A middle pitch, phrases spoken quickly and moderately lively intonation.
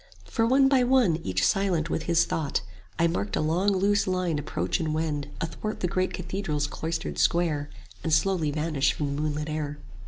No: medium, 165 Hz; average, 190 wpm; average, 3.9 semitones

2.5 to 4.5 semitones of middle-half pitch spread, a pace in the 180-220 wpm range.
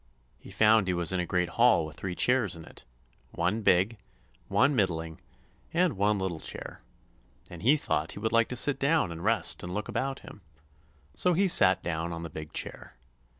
No: wide, 5.6 semitones; average, 195 wpm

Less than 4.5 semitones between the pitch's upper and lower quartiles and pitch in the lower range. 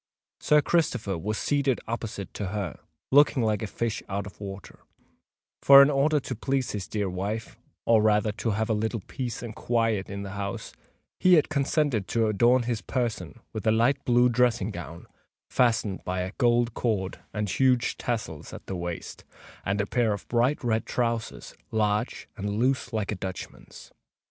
Yes: average, 3.3 semitones; low, 110 Hz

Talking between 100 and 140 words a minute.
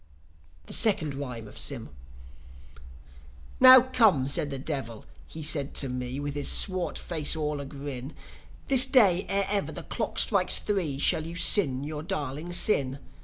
No: average, 160 wpm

